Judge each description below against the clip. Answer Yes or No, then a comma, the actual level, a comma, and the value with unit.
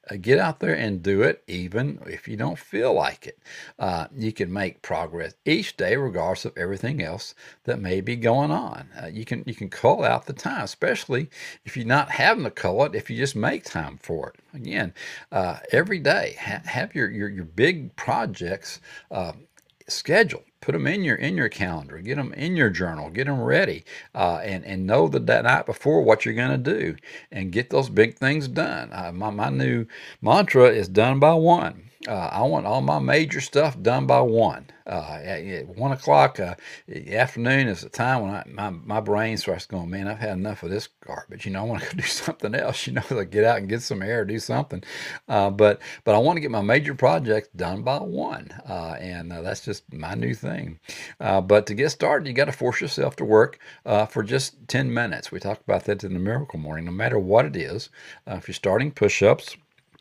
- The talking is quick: Yes, fast, 220 wpm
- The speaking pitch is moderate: No, low, 105 Hz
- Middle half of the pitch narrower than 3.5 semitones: No, average, 4.7 semitones